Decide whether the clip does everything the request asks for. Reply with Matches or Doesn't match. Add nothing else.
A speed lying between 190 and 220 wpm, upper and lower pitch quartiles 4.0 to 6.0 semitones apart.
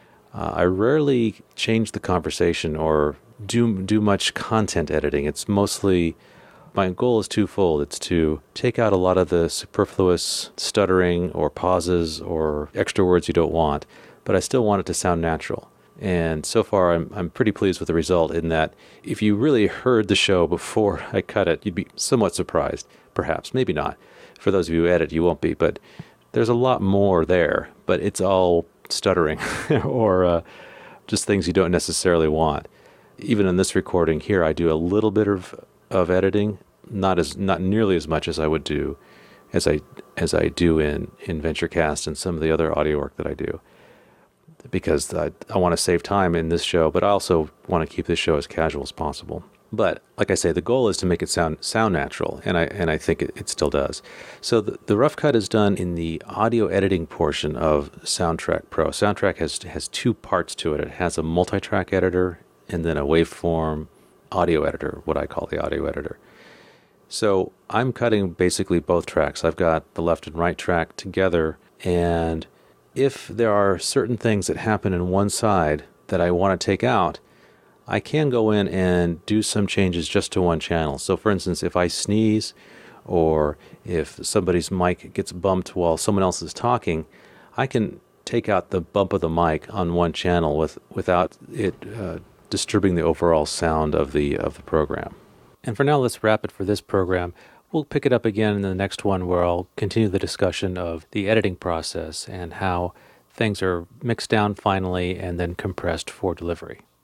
Doesn't match